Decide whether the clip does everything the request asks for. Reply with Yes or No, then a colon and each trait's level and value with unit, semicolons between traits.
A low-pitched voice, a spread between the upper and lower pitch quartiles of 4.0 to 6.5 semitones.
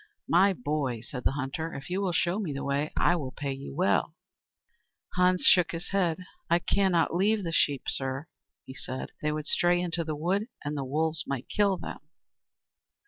No: medium, 165 Hz; average, 4.4 semitones